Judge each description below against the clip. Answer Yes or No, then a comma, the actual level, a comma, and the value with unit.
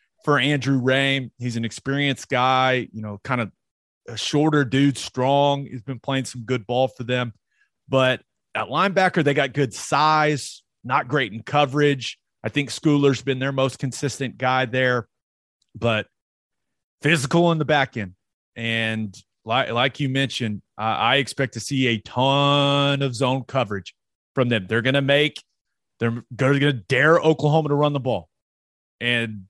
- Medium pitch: No, low, 130 Hz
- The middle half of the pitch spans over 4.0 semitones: No, average, 3.3 semitones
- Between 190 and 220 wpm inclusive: No, average, 160 wpm